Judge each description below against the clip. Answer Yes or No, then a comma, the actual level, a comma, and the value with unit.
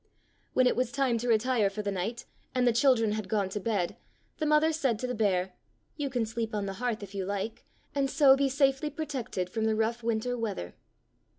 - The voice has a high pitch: Yes, high, 230 Hz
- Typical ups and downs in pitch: Yes, average, 3.9 semitones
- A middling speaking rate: No, fast, 215 wpm